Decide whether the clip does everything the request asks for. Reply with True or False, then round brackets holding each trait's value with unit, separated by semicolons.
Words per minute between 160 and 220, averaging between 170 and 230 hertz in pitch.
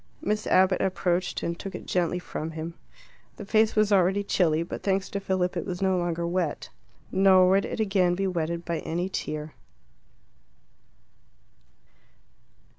False (150 wpm; 185 Hz)